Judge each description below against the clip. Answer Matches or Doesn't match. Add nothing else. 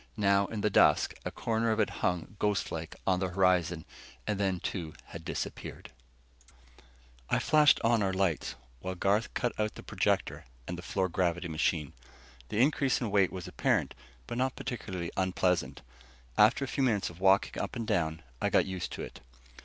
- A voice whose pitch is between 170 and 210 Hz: Doesn't match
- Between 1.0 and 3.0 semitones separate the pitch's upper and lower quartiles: Doesn't match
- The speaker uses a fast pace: Doesn't match